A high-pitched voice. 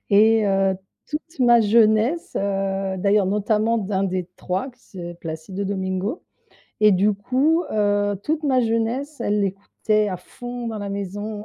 Yes: high, 210 Hz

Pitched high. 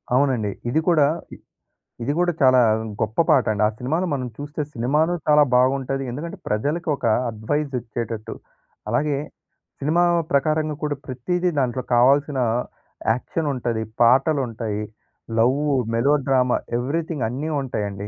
No: low, 135 Hz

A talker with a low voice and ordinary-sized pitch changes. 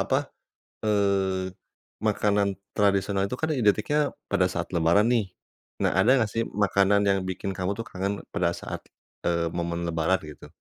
No: low, 100 Hz; narrow, 2.1 semitones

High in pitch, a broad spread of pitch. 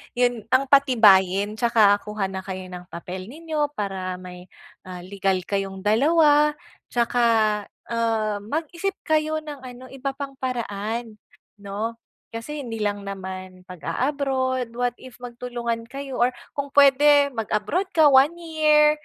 Yes: high, 240 Hz; wide, 5.7 semitones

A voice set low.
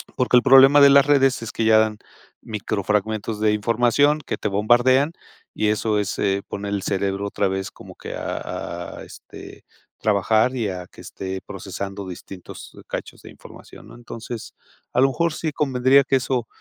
Yes: low, 110 Hz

